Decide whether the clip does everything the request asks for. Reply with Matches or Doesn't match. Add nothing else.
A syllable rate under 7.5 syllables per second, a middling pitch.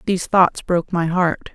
Matches